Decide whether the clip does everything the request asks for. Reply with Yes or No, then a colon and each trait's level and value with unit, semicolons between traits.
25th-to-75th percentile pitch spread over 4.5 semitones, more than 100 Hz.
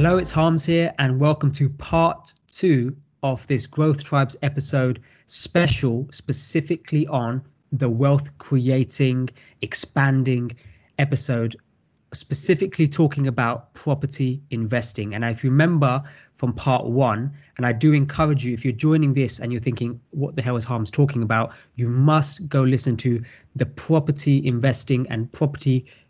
No: average, 2.9 semitones; low, 135 Hz